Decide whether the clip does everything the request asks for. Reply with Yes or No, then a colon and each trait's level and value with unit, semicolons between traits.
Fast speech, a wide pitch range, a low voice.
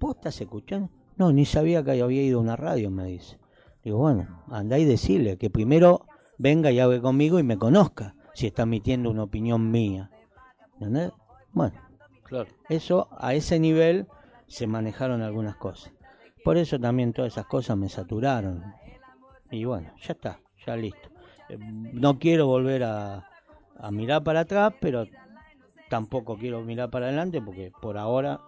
No: average, 160 wpm; wide, 6.0 semitones; low, 125 Hz